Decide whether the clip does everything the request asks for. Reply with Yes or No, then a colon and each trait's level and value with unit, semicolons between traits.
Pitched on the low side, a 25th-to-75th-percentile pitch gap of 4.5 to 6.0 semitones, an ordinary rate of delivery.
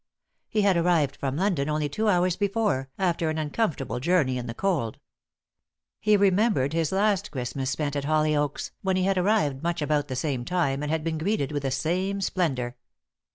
No: medium, 160 Hz; average, 5.2 semitones; average, 185 wpm